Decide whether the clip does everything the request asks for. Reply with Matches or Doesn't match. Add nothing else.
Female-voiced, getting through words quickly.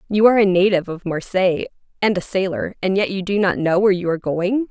Matches